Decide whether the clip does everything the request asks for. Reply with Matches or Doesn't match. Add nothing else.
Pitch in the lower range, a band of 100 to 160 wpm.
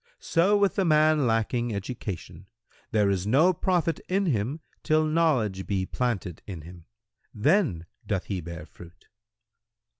Matches